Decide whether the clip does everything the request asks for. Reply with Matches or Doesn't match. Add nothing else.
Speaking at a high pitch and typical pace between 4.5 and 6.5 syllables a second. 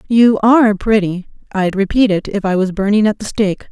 Matches